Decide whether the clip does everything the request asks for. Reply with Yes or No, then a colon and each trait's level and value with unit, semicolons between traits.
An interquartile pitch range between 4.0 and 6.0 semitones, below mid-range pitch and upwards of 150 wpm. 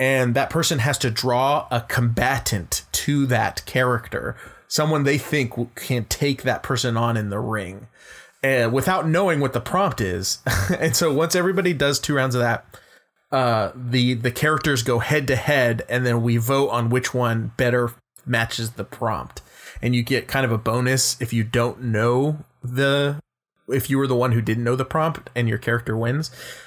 No: average, 2.8 semitones; low, 125 Hz; average, 185 wpm